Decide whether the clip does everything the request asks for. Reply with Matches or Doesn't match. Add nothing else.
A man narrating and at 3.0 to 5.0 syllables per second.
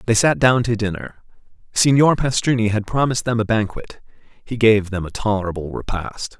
Doesn't match